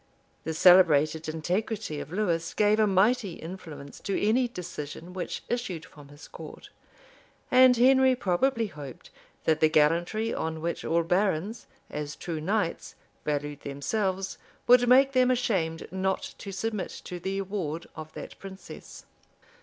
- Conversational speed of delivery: Yes, average, 145 wpm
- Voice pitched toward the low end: No, medium, 185 Hz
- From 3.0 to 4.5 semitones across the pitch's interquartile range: No, average, 5.3 semitones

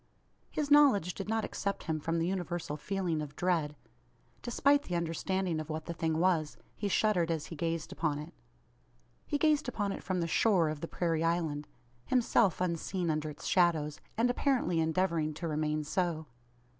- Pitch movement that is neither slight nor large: Yes, average, 3.6 semitones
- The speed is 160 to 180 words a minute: Yes, average, 175 wpm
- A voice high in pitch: No, medium, 170 Hz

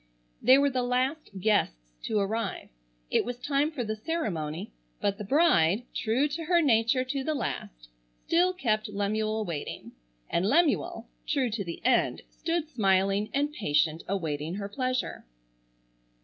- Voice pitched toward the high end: Yes, high, 225 Hz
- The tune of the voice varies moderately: No, wide, 6.1 semitones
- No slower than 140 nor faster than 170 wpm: Yes, average, 150 wpm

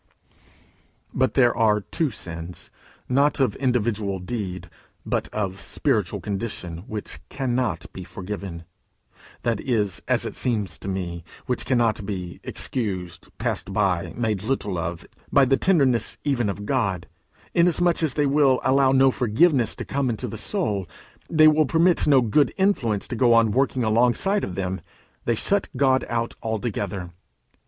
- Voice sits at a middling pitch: No, low, 115 Hz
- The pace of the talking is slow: No, average, 150 wpm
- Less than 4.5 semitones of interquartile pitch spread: No, average, 5.3 semitones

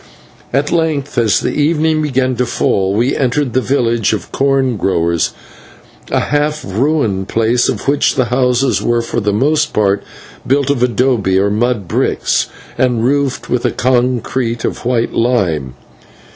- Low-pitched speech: Yes, low, 125 Hz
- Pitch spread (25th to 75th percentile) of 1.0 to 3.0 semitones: No, average, 3.7 semitones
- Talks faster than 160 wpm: No, average, 155 wpm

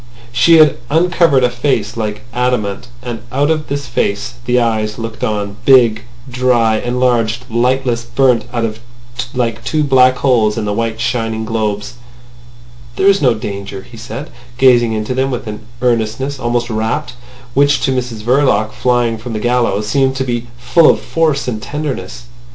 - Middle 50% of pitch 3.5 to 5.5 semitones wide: No, average, 2.9 semitones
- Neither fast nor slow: Yes, average, 160 wpm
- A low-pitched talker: Yes, low, 120 Hz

